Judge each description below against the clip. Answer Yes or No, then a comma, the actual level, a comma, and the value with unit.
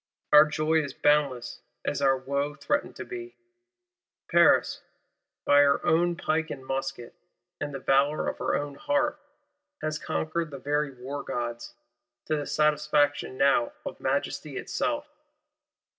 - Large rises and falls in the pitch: No, narrow, 2.6 semitones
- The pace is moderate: No, slow, 130 wpm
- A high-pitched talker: No, medium, 145 Hz